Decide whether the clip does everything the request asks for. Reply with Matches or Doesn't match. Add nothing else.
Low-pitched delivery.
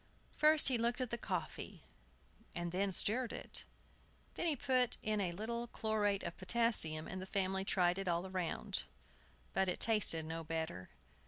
Doesn't match